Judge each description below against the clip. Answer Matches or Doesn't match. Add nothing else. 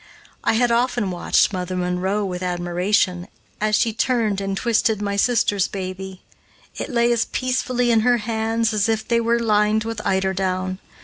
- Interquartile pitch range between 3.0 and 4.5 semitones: Matches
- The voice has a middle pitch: Doesn't match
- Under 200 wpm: Matches